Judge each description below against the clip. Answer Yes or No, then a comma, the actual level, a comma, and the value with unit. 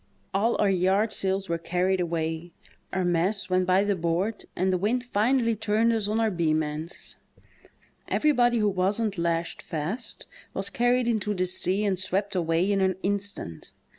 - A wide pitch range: No, average, 3.4 semitones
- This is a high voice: Yes, high, 195 Hz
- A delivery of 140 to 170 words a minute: Yes, average, 165 wpm